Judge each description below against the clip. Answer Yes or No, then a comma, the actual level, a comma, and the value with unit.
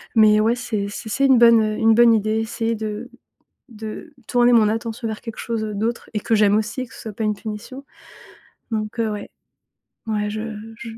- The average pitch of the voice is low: No, high, 220 Hz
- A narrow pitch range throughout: Yes, narrow, 1.6 semitones